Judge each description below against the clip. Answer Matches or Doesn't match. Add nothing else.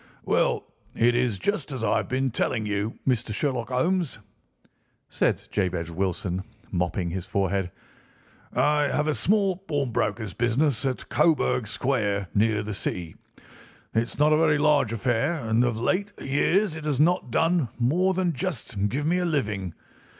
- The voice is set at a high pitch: Doesn't match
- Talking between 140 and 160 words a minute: Matches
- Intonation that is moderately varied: Doesn't match